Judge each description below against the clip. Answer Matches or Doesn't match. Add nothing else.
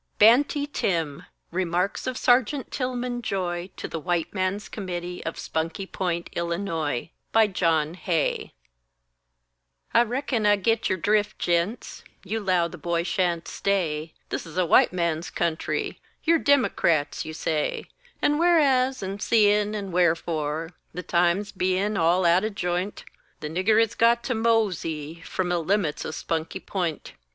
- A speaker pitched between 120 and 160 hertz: Doesn't match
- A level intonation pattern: Doesn't match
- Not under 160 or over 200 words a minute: Doesn't match